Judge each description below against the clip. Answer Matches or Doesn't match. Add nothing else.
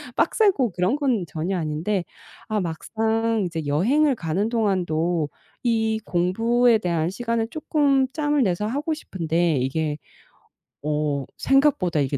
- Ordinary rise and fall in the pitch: Doesn't match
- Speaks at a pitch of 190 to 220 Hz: Matches